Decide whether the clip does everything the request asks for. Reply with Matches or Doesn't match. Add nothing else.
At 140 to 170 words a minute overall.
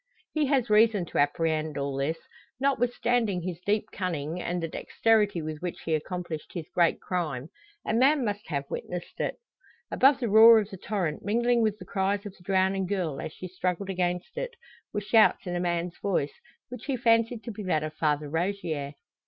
Doesn't match